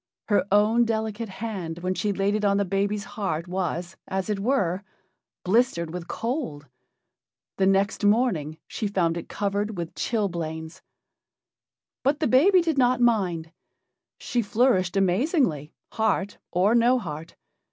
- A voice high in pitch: Yes, high, 200 Hz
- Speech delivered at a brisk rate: No, average, 140 wpm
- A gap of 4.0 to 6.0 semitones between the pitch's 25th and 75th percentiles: Yes, average, 4.6 semitones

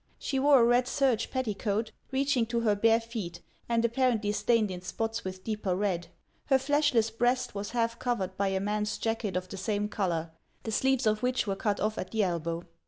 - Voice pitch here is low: No, high, 220 Hz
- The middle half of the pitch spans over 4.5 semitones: No, average, 3.3 semitones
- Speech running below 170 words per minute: No, average, 200 wpm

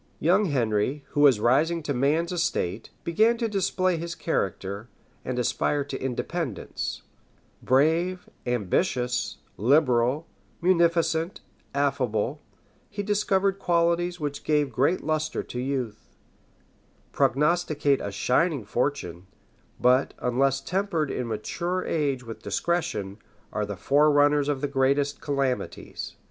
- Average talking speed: No, slow, 115 wpm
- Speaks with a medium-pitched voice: Yes, medium, 145 Hz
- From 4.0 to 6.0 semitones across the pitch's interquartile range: Yes, average, 5.2 semitones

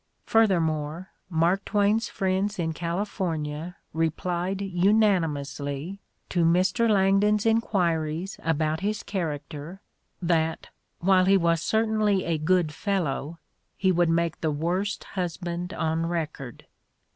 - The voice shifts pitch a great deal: No, average, 3.4 semitones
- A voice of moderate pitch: Yes, medium, 175 Hz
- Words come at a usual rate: No, slow, 120 wpm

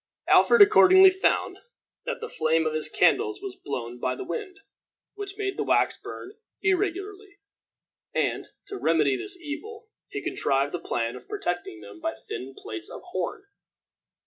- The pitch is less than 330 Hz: No, very high, 370 Hz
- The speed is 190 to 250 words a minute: No, average, 155 wpm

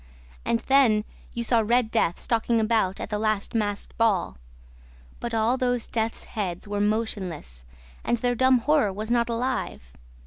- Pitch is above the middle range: Yes, high, 225 Hz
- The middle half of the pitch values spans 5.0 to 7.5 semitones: No, narrow, 2.5 semitones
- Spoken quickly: No, average, 160 wpm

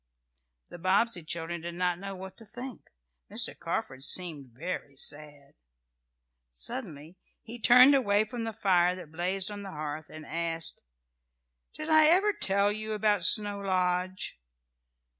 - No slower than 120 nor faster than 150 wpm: Yes, average, 140 wpm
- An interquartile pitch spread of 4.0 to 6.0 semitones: Yes, average, 4.7 semitones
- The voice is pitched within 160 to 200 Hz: Yes, medium, 185 Hz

